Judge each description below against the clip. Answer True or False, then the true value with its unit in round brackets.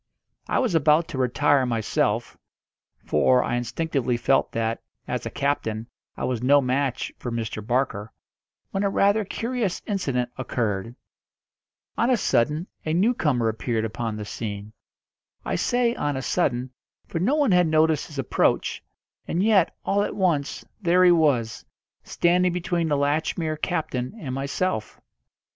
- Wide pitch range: True (6.6 semitones)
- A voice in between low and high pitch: True (145 Hz)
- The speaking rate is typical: True (150 wpm)